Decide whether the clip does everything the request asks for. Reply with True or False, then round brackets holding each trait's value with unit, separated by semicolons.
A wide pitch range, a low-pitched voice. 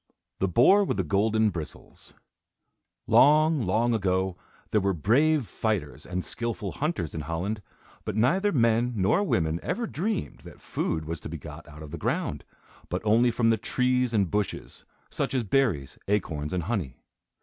True (6.3 semitones; 105 Hz)